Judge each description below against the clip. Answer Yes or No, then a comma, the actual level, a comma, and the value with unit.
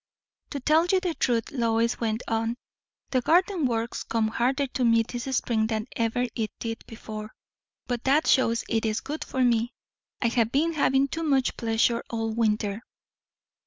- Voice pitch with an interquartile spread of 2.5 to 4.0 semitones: Yes, average, 3.0 semitones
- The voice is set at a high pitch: Yes, high, 235 Hz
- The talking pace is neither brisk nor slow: Yes, average, 165 wpm